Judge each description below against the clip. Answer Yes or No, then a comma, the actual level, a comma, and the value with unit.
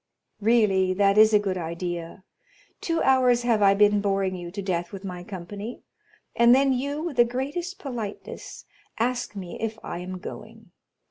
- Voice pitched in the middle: No, high, 210 Hz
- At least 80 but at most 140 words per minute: No, average, 160 wpm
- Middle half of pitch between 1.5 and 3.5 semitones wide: No, average, 4.8 semitones